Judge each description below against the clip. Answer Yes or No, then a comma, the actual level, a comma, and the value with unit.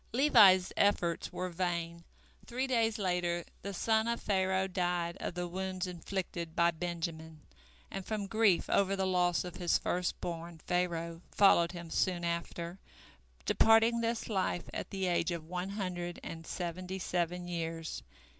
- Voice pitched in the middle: Yes, medium, 180 Hz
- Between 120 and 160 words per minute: Yes, average, 150 wpm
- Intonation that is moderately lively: No, narrow, 2.2 semitones